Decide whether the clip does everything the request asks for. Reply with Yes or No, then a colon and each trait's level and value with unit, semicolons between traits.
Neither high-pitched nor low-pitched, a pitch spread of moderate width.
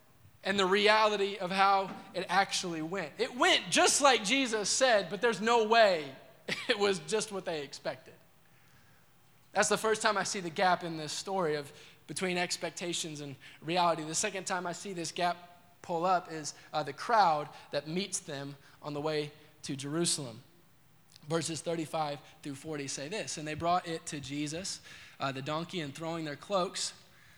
Yes: medium, 170 Hz; average, 4.4 semitones